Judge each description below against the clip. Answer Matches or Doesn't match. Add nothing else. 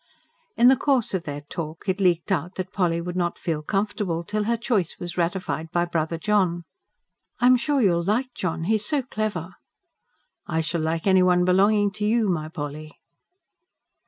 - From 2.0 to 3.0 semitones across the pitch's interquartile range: Doesn't match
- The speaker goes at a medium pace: Matches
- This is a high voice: Doesn't match